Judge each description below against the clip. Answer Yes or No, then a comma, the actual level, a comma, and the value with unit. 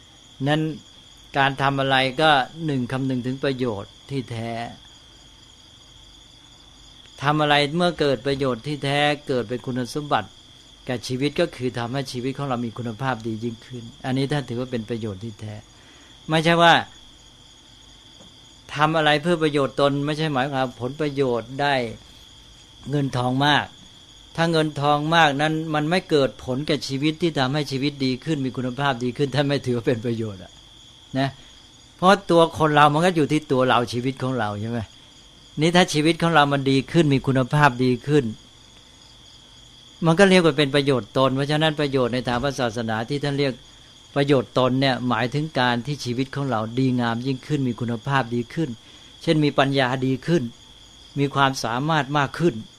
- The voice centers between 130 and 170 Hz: Yes, low, 135 Hz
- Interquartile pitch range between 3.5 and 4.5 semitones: No, average, 3.0 semitones